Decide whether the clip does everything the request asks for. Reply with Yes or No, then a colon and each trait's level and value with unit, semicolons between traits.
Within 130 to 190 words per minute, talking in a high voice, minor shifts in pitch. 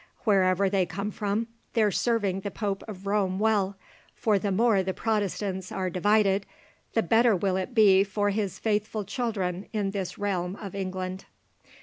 Yes: average, 160 wpm; high, 200 Hz; narrow, 2.0 semitones